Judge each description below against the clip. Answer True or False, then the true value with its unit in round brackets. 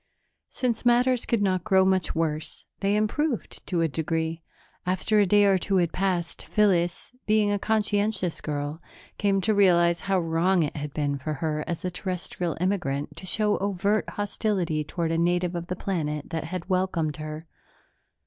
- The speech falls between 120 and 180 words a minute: True (170 wpm)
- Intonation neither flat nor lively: True (3.8 semitones)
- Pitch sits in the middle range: True (180 Hz)